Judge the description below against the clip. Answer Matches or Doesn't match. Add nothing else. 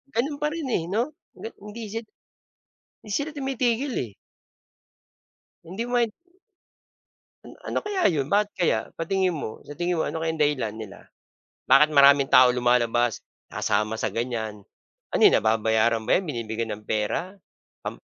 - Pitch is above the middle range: Doesn't match